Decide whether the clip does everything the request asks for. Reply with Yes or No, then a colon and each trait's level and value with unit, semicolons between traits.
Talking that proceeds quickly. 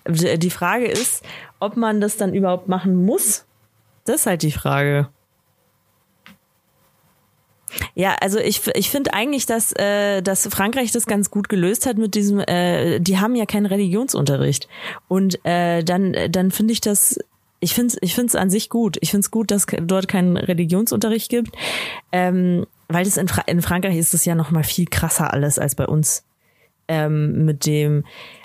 No: average, 175 wpm